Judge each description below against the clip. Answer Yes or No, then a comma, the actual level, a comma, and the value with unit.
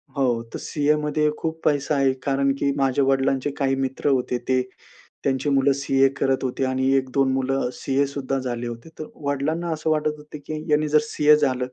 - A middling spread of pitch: No, narrow, 2.0 semitones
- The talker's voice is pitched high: No, low, 135 Hz